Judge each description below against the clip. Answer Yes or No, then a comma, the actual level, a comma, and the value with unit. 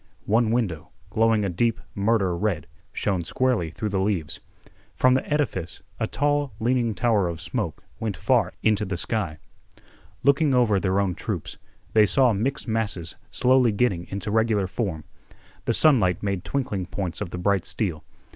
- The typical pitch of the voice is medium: No, low, 105 Hz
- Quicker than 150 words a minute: Yes, average, 160 wpm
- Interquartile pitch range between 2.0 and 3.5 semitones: No, average, 4.2 semitones